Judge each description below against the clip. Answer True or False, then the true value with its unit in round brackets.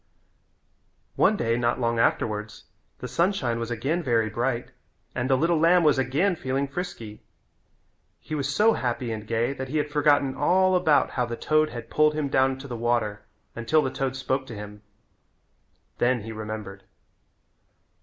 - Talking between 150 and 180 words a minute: True (165 wpm)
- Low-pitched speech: True (130 Hz)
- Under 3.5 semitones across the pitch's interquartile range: False (4.5 semitones)